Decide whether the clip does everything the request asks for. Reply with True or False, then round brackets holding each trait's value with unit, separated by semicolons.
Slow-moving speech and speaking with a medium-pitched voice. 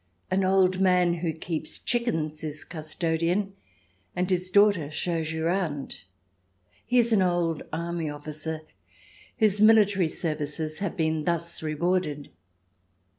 True (125 wpm; 170 Hz)